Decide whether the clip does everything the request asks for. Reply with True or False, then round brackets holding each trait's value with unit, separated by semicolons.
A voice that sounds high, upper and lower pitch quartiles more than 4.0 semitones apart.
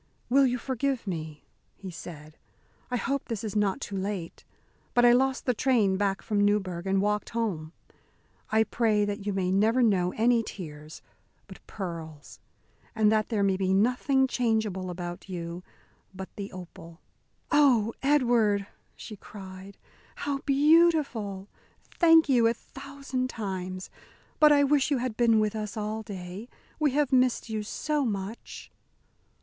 True (215 Hz; 4.8 semitones)